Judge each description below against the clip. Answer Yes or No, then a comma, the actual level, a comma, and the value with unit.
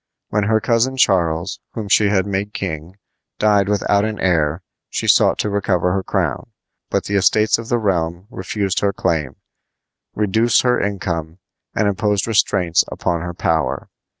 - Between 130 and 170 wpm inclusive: Yes, average, 155 wpm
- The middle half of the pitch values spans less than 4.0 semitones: Yes, average, 3.3 semitones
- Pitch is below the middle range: Yes, low, 100 Hz